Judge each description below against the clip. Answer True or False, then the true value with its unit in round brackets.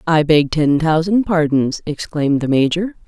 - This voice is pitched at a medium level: True (160 Hz)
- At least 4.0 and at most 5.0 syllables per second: True (4.6 syllables/s)